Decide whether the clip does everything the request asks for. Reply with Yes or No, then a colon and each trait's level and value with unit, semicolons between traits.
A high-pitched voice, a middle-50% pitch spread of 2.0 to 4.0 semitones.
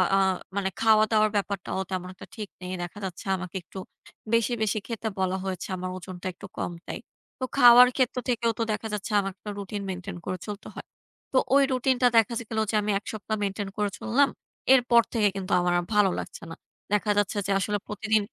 Yes: high, 210 Hz; average, 3.0 semitones